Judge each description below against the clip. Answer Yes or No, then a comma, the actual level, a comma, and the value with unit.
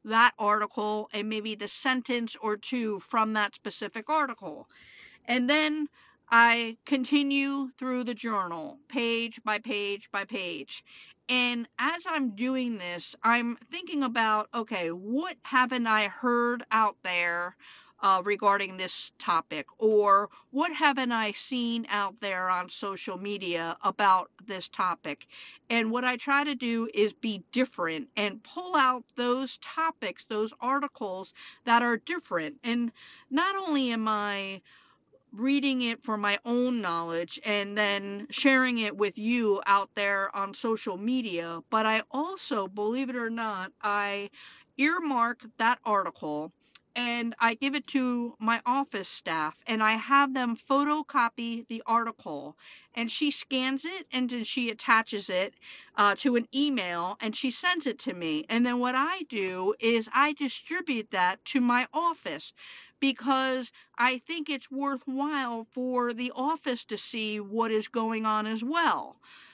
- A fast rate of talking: No, average, 145 wpm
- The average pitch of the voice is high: Yes, high, 235 Hz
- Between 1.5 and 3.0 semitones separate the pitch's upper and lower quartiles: No, average, 4.1 semitones